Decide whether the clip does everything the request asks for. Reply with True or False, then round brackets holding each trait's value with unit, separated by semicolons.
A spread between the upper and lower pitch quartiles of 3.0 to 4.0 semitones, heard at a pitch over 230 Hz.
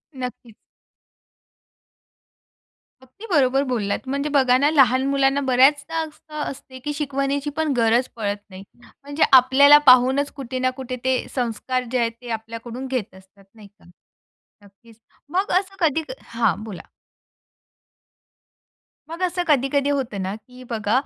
True (3.5 semitones; 260 Hz)